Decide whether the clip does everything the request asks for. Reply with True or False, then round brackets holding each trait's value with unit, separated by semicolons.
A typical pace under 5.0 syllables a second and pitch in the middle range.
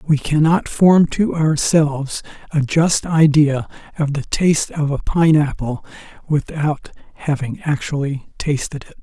True (4.2 syllables/s; 150 Hz)